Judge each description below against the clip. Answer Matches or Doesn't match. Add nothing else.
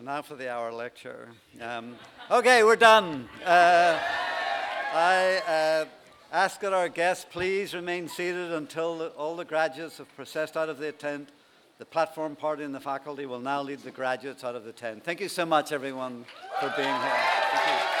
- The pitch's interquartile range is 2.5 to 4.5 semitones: Matches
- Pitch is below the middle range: Doesn't match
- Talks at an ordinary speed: Matches